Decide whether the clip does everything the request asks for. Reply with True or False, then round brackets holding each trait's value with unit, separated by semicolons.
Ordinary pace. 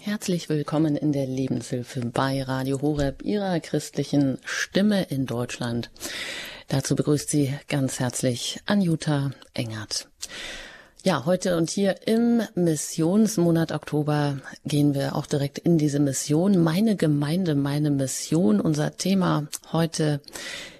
False (120 wpm)